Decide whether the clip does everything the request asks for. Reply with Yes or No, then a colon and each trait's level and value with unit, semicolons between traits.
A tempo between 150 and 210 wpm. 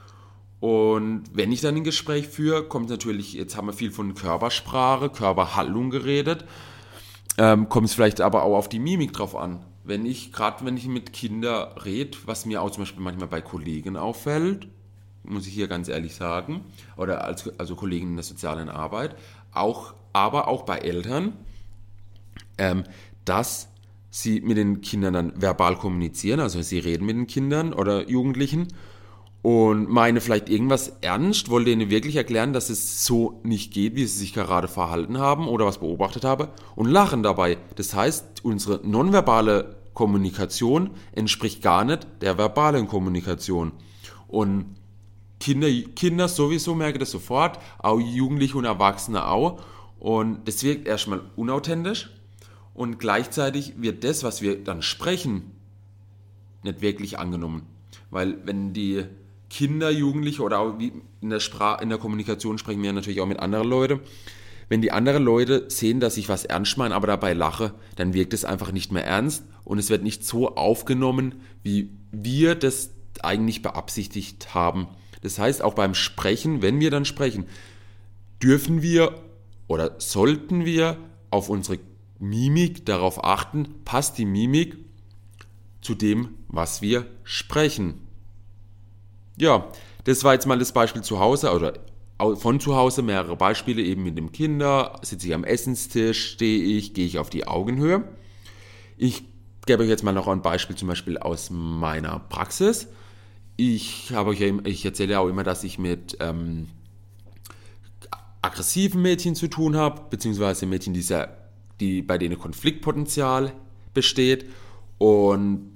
Yes: average, 155 wpm